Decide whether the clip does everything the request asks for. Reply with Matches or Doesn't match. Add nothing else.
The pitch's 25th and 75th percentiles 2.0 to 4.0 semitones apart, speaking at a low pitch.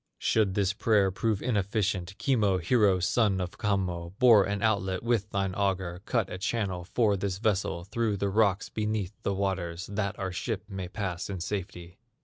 Matches